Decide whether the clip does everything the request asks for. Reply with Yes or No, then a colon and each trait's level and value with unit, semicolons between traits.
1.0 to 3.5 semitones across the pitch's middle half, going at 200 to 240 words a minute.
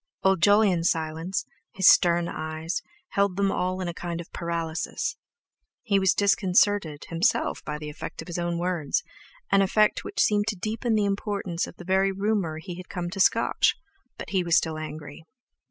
No: average, 3.2 semitones; average, 175 wpm